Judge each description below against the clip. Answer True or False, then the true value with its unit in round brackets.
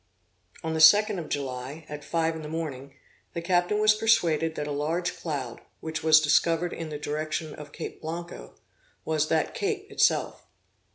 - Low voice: False (160 Hz)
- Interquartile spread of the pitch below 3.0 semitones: True (2.5 semitones)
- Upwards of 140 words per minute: True (170 wpm)